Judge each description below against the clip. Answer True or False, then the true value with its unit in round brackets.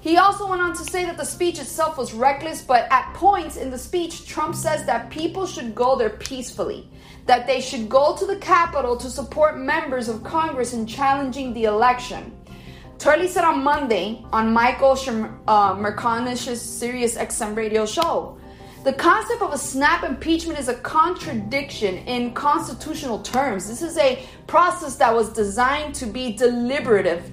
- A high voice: True (270 Hz)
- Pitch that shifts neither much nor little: True (5.0 semitones)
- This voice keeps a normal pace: True (170 wpm)